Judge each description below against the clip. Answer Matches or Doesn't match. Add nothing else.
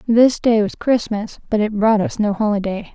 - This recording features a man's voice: Doesn't match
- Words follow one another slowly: Doesn't match